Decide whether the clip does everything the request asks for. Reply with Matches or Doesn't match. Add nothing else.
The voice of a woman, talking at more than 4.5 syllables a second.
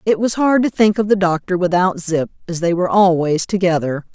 Matches